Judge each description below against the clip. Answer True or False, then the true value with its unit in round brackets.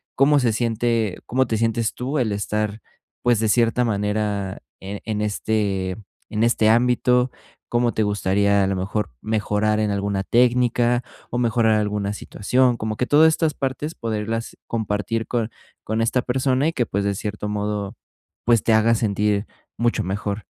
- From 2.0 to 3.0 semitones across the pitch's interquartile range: True (2.7 semitones)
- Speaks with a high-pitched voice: False (110 Hz)